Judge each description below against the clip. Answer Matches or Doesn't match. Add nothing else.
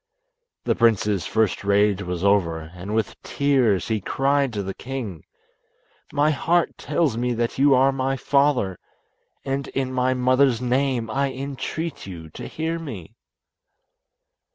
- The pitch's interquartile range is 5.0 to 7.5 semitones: Matches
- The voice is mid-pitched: Doesn't match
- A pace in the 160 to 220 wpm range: Doesn't match